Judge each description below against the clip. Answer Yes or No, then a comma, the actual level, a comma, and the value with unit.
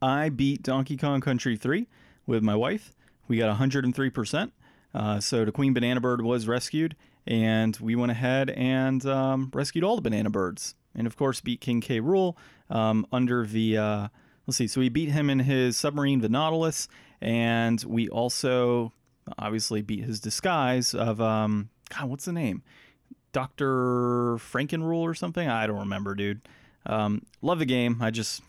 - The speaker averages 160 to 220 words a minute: Yes, average, 170 wpm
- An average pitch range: Yes, average, 3.3 semitones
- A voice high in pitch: No, low, 125 Hz